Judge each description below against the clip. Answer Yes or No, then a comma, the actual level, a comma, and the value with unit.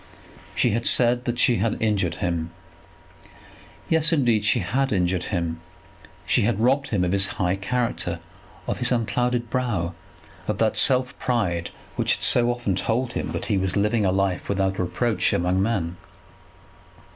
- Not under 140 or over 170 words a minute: Yes, average, 160 wpm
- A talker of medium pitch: No, low, 105 Hz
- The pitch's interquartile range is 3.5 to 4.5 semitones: No, average, 4.9 semitones